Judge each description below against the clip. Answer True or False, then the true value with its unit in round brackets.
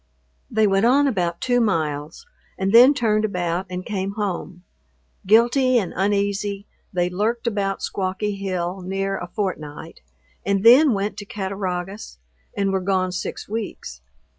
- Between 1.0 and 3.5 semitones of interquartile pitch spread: True (2.8 semitones)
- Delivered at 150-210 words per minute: False (140 wpm)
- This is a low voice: False (195 Hz)